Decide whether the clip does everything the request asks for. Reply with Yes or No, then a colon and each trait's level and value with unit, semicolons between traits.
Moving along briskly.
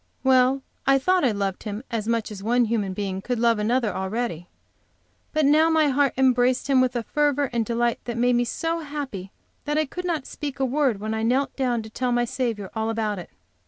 Yes: fast, 220 wpm